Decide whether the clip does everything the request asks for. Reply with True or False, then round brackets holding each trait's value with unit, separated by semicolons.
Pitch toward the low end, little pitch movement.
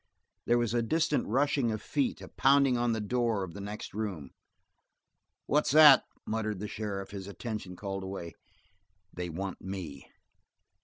False (105 Hz; 4.0 semitones)